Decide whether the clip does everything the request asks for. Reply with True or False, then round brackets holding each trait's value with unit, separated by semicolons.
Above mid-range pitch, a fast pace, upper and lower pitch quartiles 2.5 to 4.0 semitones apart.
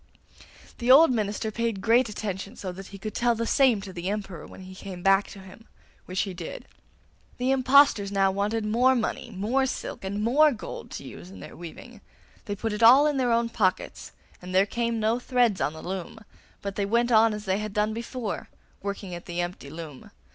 True (210 Hz; 210 wpm; 3.7 semitones)